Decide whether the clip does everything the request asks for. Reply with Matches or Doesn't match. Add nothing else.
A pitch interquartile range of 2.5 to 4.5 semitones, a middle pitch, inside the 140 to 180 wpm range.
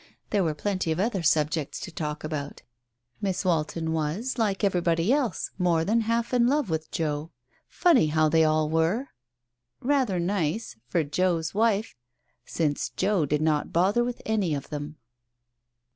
Doesn't match